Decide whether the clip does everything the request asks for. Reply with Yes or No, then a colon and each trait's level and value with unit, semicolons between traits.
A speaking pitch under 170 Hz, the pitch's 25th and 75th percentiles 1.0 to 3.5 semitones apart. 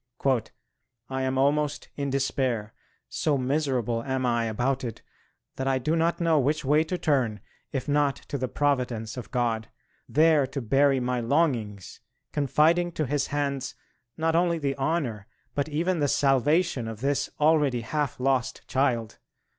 Yes: low, 135 Hz; average, 3.0 semitones